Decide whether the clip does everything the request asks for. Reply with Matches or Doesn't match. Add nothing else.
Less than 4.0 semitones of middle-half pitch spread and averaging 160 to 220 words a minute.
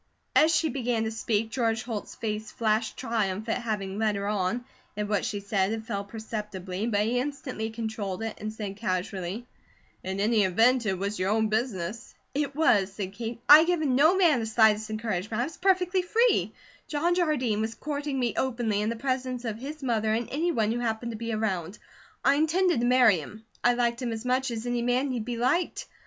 Matches